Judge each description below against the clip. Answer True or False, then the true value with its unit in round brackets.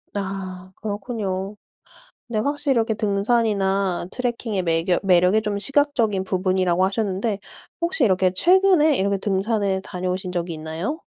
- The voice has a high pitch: True (200 Hz)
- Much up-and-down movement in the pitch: False (3.5 semitones)